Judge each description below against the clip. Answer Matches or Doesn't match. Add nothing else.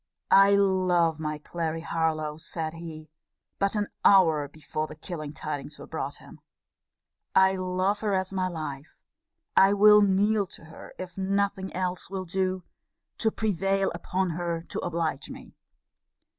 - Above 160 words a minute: Doesn't match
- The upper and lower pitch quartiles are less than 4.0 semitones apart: Matches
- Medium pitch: Matches